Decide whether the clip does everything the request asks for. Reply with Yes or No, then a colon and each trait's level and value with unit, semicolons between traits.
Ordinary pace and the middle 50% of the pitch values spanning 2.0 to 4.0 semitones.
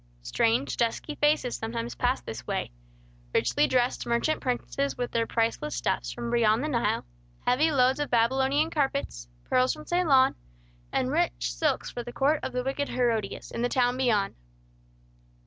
Yes: average, 160 wpm; average, 3.1 semitones